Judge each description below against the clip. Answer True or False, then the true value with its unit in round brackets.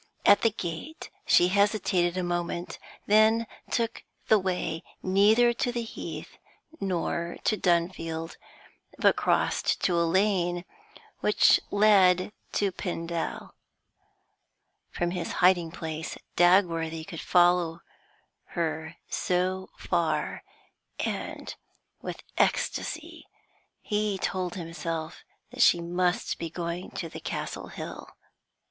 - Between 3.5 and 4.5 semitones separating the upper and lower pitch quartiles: False (2.8 semitones)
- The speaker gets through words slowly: True (110 wpm)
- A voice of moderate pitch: True (180 Hz)